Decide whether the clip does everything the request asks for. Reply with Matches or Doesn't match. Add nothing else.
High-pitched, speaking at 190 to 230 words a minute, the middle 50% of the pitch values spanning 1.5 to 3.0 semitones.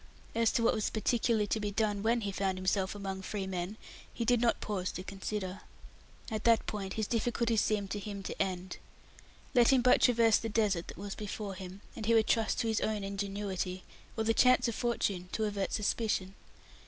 Matches